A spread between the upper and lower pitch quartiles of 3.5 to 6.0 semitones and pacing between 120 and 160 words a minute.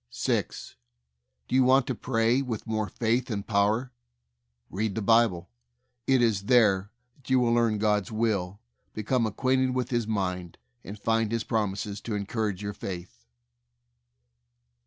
No: average, 2.9 semitones; average, 155 wpm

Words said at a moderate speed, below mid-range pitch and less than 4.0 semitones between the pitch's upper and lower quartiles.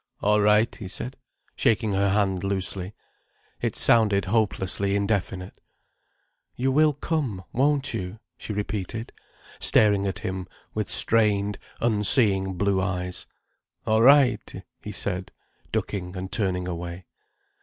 No: slow, 120 wpm; low, 100 Hz; average, 2.8 semitones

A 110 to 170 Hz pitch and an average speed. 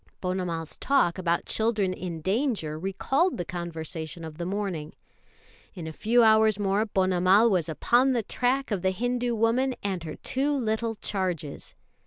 No: high, 195 Hz; average, 155 wpm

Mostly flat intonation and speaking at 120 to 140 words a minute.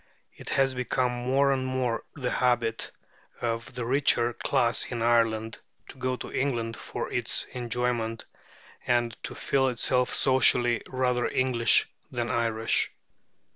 Yes: narrow, 1.7 semitones; slow, 135 wpm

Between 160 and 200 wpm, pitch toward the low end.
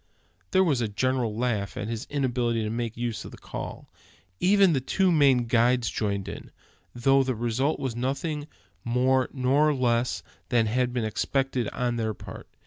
Yes: average, 170 wpm; low, 125 Hz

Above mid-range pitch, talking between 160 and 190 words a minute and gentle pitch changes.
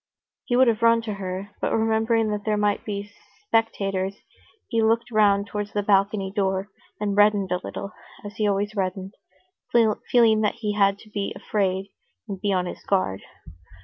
Yes: high, 205 Hz; average, 175 wpm; narrow, 1.9 semitones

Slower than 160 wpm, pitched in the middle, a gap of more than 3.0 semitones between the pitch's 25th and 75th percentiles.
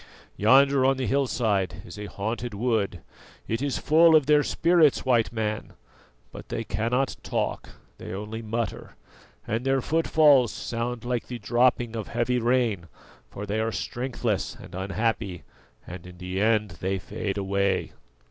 No: average, 150 wpm; low, 115 Hz; average, 4.0 semitones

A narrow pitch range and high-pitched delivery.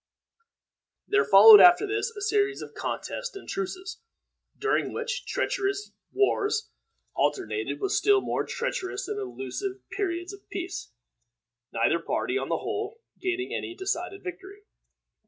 Yes: narrow, 1.9 semitones; very high, 395 Hz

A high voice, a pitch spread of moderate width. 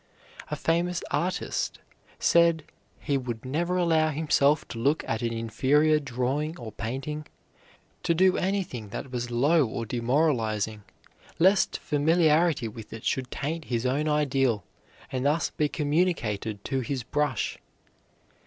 No: medium, 145 Hz; average, 4.9 semitones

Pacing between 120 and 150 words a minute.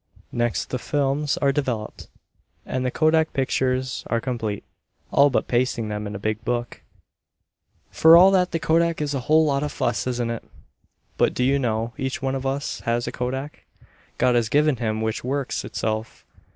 No: average, 180 wpm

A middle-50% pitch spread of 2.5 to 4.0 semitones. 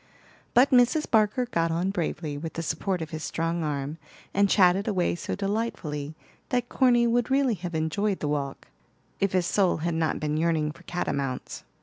No: average, 5.1 semitones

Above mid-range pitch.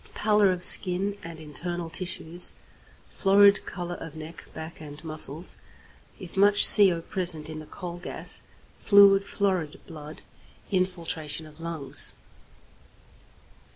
No: medium, 175 Hz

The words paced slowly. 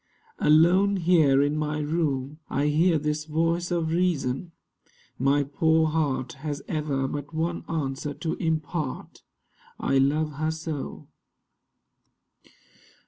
Yes: slow, 115 wpm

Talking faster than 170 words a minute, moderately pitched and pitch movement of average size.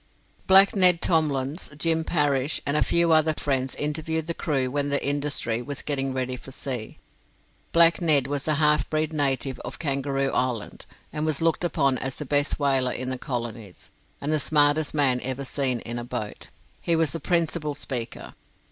Yes: average, 180 wpm; medium, 145 Hz; average, 3.1 semitones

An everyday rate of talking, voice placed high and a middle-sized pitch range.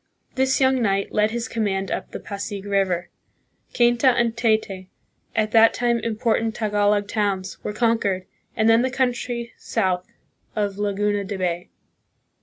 Yes: average, 155 wpm; high, 215 Hz; average, 3.0 semitones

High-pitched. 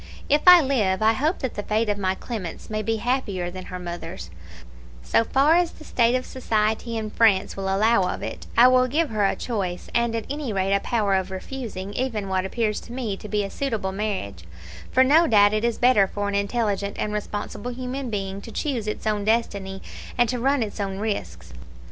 Yes: high, 215 Hz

